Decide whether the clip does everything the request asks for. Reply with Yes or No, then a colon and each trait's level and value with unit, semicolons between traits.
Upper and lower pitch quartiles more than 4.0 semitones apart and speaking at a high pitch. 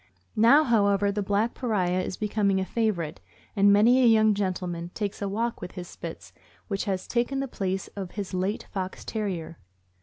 No: average, 2.9 semitones; high, 200 Hz